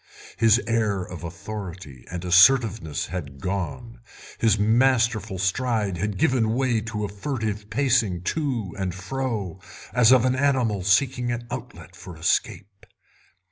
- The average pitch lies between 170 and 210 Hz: No, low, 105 Hz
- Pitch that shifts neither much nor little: Yes, average, 4.4 semitones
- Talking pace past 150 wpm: No, slow, 135 wpm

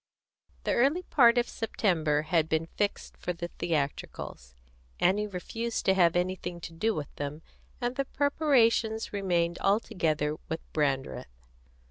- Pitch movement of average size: No, wide, 6.2 semitones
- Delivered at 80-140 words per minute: Yes, slow, 135 wpm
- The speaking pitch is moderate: Yes, medium, 180 Hz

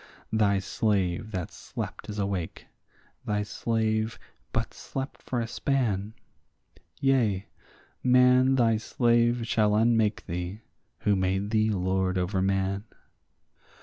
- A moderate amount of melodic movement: Yes, average, 3.3 semitones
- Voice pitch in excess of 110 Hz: No, low, 105 Hz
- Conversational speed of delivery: No, slow, 115 wpm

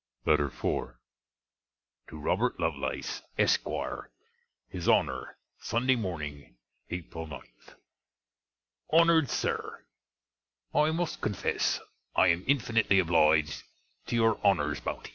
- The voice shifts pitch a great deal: Yes, wide, 7.6 semitones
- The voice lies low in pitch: Yes, very low, 90 Hz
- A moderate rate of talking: No, slow, 100 wpm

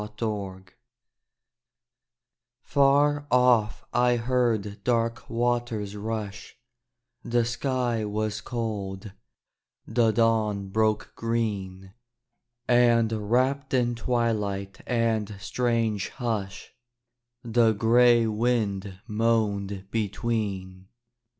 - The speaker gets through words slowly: Yes, slow, 80 wpm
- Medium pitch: No, low, 115 Hz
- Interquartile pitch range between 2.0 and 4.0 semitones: Yes, average, 2.7 semitones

